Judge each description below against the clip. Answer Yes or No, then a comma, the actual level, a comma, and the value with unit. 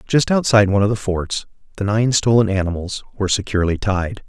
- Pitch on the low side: Yes, low, 100 Hz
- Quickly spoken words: No, average, 180 wpm